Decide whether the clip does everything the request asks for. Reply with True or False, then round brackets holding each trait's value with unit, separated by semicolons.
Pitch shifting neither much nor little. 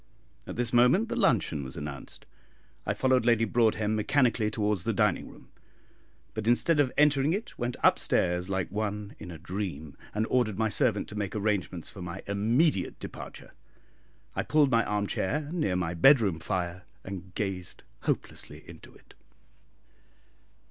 True (4.7 semitones)